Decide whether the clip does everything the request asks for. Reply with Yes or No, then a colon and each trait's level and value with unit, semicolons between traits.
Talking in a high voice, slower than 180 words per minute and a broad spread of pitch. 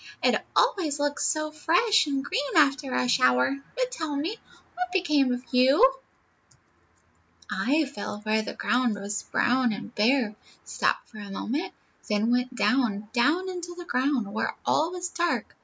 Yes: very high, 275 Hz; average, 155 wpm; wide, 6.0 semitones